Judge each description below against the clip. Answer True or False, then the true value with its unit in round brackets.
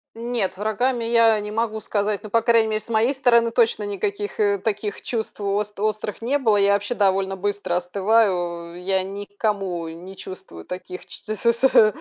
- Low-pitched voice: False (210 Hz)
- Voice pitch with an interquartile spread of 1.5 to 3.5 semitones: True (2.6 semitones)